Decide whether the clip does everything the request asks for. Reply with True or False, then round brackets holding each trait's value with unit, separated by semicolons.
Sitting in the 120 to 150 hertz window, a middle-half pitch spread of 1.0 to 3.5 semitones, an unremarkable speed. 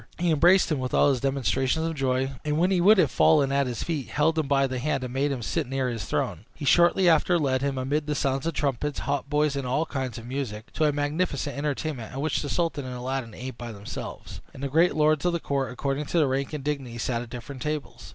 False (140 Hz; 2.8 semitones; 250 wpm)